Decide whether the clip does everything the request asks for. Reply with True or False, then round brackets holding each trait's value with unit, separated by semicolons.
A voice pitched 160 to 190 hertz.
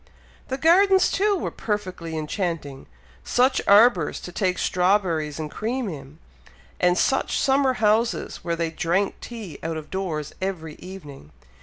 True (185 Hz)